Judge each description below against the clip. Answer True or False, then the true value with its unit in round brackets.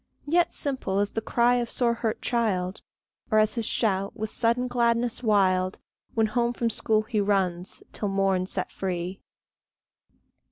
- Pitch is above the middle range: True (215 Hz)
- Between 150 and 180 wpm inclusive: True (155 wpm)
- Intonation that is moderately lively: True (3.4 semitones)